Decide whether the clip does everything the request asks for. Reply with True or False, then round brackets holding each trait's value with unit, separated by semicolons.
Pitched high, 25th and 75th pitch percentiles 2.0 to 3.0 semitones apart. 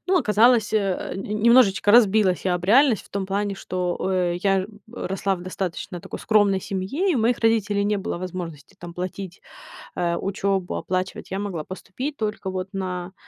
True (195 Hz; 2.6 semitones)